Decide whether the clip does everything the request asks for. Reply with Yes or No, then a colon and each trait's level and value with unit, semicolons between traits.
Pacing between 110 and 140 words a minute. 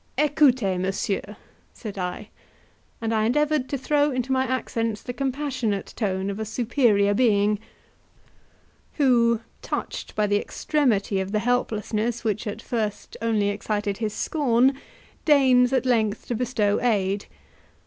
Yes: slow, 135 wpm